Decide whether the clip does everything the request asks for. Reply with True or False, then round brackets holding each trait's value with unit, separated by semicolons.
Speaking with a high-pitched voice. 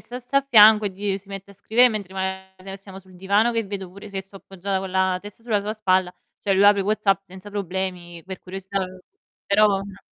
True (195 Hz)